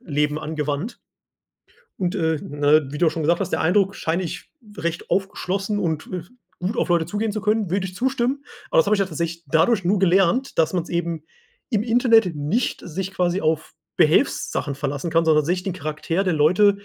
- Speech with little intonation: No, average, 3.9 semitones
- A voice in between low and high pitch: Yes, medium, 175 Hz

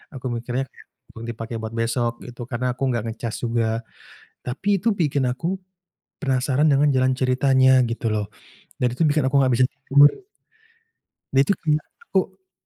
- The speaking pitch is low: Yes, low, 130 Hz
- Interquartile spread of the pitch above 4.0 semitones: No, average, 3.1 semitones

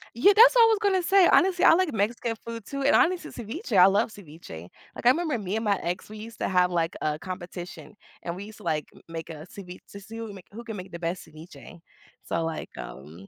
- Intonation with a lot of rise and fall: Yes, wide, 5.8 semitones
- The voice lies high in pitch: Yes, high, 200 Hz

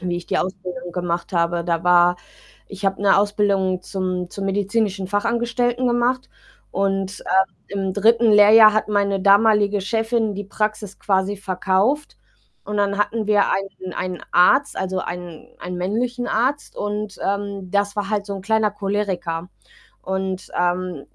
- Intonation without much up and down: Yes, narrow, 2.3 semitones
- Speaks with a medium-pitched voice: No, high, 200 Hz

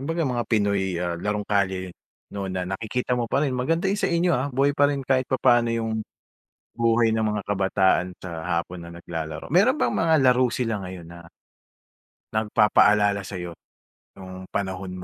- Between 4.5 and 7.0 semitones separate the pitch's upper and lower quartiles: Yes, wide, 5.4 semitones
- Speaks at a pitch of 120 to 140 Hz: No, low, 105 Hz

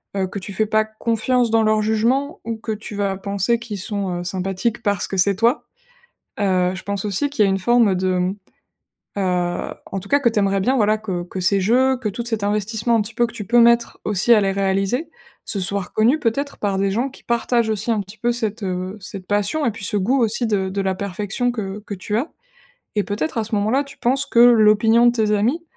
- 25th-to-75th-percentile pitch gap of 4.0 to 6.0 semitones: No, average, 3.2 semitones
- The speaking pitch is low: No, high, 210 Hz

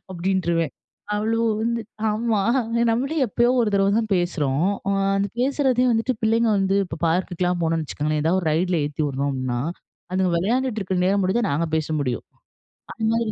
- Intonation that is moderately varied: No, wide, 5.7 semitones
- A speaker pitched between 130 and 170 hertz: No, high, 190 Hz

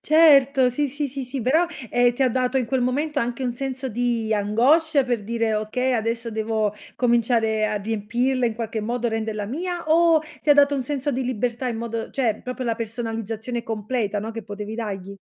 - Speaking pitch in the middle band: No, high, 240 Hz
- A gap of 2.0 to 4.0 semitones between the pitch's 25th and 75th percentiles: Yes, average, 3.0 semitones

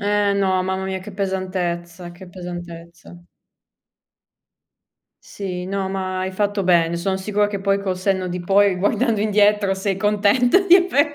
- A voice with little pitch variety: Yes, narrow, 2.0 semitones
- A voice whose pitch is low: No, high, 190 Hz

